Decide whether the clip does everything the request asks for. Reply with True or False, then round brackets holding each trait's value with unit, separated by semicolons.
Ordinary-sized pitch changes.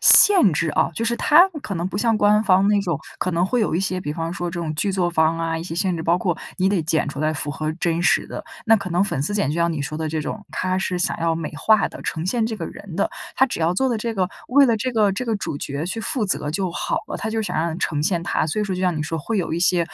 True (4.1 semitones)